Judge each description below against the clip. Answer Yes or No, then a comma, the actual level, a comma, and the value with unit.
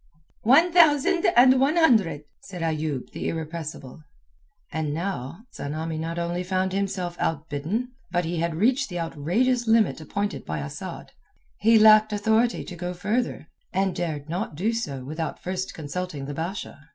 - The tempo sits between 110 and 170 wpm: Yes, average, 150 wpm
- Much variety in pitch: Yes, wide, 5.8 semitones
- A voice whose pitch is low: No, medium, 180 Hz